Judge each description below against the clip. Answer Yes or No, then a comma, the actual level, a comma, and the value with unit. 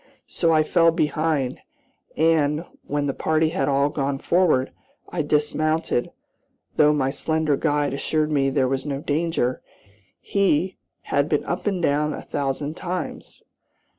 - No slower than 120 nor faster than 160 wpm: Yes, average, 140 wpm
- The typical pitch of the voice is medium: Yes, medium, 150 Hz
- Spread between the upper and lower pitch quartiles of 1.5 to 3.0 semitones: Yes, narrow, 2.4 semitones